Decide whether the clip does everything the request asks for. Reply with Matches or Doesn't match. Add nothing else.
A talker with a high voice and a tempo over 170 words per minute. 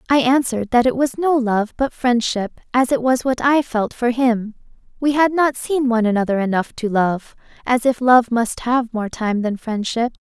Matches